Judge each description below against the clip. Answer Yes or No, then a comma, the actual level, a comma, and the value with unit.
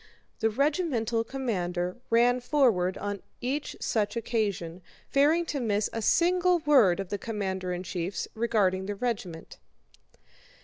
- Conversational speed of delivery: No, slow, 130 wpm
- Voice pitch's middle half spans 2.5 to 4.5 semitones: No, wide, 5.6 semitones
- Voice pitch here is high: Yes, high, 220 Hz